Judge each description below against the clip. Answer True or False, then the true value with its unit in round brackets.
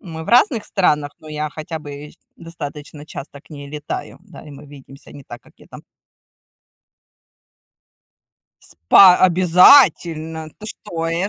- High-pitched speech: False (160 Hz)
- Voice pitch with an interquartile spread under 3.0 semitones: False (3.4 semitones)